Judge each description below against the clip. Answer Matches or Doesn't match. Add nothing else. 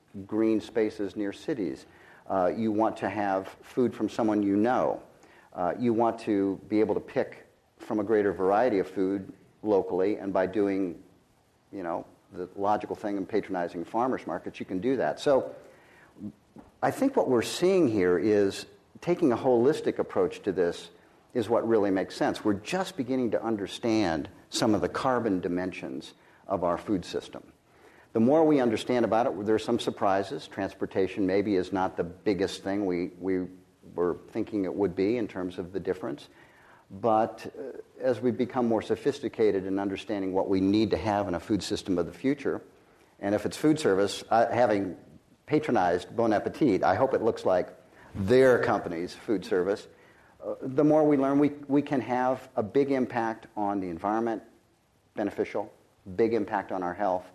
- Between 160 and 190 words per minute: Matches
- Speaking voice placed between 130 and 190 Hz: Doesn't match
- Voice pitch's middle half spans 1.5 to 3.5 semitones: Doesn't match